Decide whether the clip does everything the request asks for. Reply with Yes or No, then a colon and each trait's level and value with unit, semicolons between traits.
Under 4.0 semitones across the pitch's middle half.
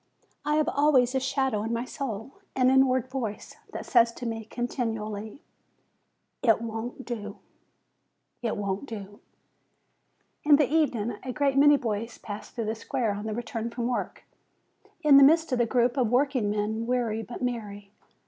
Yes: average, 3.3 semitones